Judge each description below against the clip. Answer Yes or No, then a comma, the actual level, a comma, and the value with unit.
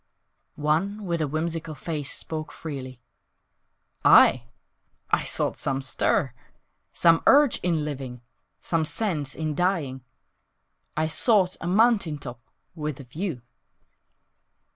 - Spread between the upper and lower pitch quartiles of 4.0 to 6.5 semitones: Yes, average, 4.3 semitones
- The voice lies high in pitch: No, medium, 155 Hz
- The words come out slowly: Yes, slow, 115 wpm